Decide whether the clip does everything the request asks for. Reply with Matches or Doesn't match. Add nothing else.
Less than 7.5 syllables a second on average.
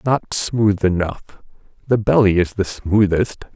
Matches